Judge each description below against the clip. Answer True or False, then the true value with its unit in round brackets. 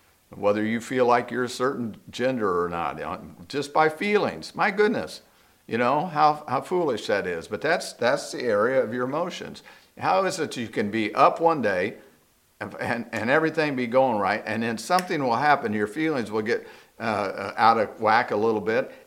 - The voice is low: False (145 Hz)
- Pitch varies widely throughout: True (7.8 semitones)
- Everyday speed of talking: True (195 wpm)